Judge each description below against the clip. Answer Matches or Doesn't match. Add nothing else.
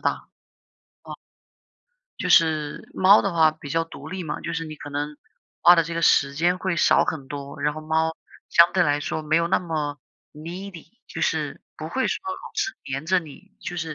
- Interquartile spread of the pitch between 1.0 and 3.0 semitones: Matches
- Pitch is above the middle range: Doesn't match